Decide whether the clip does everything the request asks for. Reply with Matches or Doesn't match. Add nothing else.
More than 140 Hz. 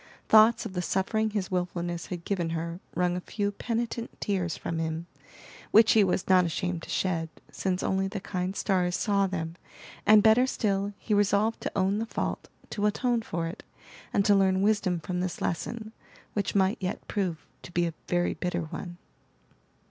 Matches